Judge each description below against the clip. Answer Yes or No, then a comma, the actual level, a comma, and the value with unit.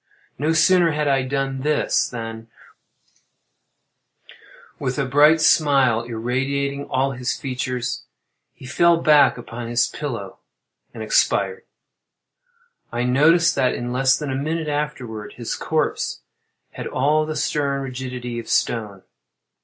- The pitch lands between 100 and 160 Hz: Yes, low, 135 Hz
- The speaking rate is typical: No, slow, 125 wpm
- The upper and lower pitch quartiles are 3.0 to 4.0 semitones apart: Yes, average, 3.5 semitones